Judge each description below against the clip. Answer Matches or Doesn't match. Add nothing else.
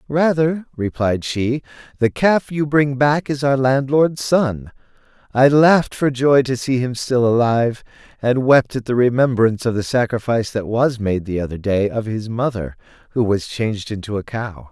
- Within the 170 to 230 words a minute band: Matches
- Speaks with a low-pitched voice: Matches